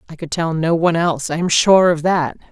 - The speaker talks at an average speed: No, fast, 265 wpm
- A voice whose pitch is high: No, medium, 165 Hz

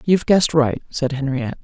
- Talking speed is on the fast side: No, average, 185 wpm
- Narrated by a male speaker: No, female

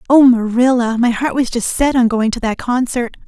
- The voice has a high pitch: Yes, high, 240 Hz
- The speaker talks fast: Yes, fast, 220 wpm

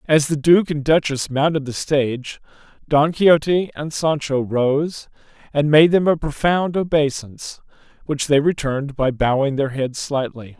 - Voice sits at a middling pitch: Yes, medium, 145 Hz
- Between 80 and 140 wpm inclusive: No, average, 155 wpm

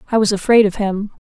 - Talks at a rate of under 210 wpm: No, fast, 235 wpm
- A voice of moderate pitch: No, high, 205 Hz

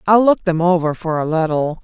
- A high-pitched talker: No, medium, 170 Hz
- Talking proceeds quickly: Yes, fast, 230 wpm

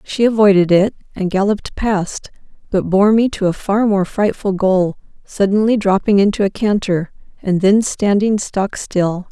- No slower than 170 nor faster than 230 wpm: No, average, 160 wpm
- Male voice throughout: No, female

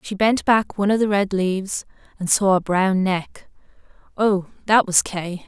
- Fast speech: No, average, 185 wpm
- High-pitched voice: Yes, high, 195 Hz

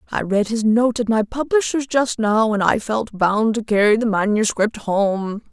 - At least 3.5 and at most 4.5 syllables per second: Yes, 4.4 syllables/s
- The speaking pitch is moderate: No, high, 220 Hz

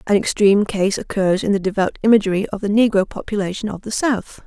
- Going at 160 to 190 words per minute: No, average, 200 wpm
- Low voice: No, high, 200 Hz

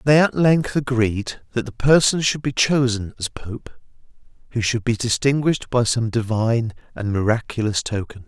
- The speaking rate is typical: Yes, average, 160 wpm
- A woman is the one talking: No, male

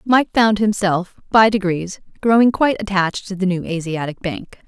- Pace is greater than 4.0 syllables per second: Yes, 5.1 syllables/s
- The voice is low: No, high, 195 Hz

